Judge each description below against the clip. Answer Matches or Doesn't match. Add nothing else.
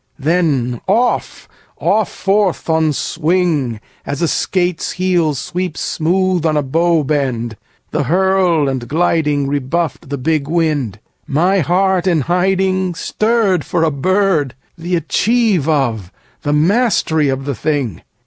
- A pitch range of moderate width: Matches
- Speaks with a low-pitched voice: Doesn't match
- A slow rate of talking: Matches